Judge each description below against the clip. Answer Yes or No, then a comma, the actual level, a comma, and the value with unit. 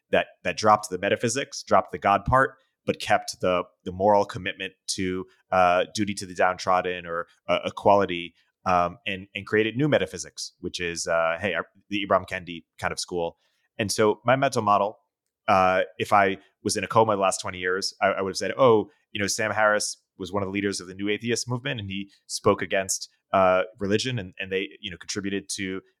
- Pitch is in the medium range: No, low, 100 Hz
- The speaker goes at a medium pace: No, fast, 210 wpm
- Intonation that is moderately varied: No, narrow, 2.2 semitones